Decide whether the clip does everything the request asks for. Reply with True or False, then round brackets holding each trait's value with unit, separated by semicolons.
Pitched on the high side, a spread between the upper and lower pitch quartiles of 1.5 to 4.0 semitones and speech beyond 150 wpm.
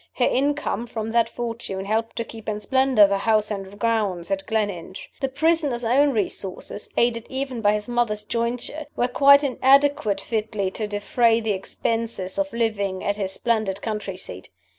True (225 Hz; 3.1 semitones; 165 wpm)